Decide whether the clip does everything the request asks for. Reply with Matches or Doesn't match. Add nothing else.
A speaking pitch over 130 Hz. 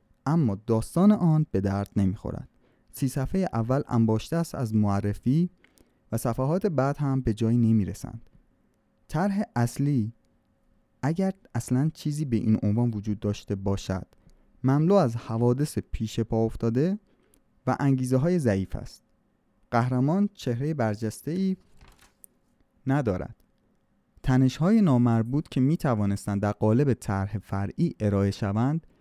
Doesn't match